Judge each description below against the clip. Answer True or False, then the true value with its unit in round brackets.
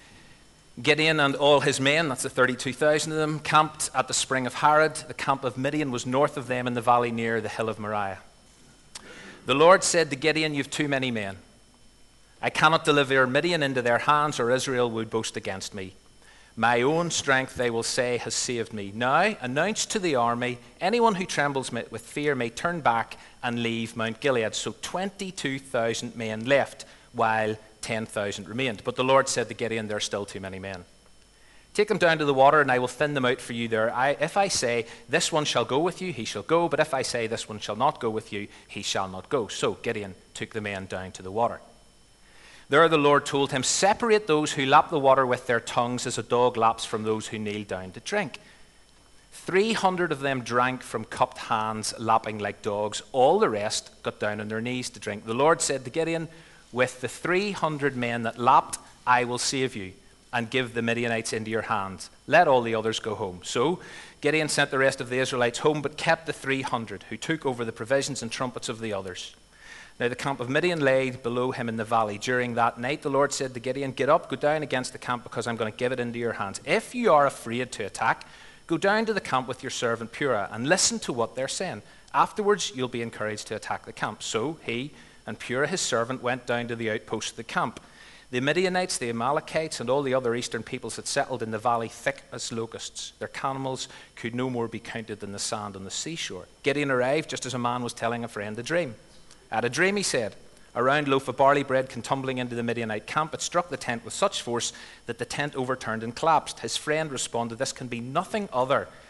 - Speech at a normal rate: False (225 wpm)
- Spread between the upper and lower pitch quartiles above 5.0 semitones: False (4.0 semitones)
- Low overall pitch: True (125 Hz)